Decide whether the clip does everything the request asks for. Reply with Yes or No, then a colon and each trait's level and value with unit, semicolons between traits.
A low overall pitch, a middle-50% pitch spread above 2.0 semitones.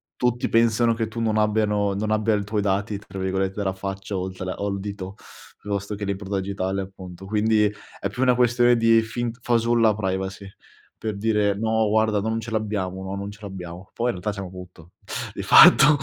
Yes: low, 105 Hz; narrow, 2.5 semitones